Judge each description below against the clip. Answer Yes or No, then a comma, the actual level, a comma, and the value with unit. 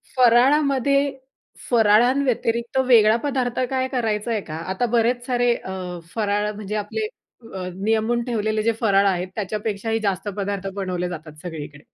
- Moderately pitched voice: No, high, 220 Hz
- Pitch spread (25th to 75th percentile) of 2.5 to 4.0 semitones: Yes, average, 3.6 semitones